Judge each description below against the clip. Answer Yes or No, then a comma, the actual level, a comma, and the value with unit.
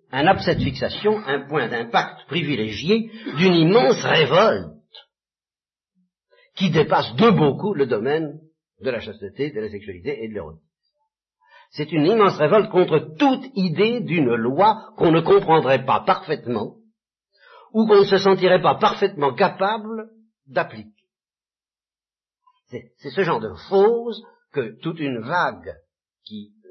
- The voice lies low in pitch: No, high, 190 Hz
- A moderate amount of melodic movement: No, wide, 6.0 semitones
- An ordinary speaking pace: No, slow, 135 wpm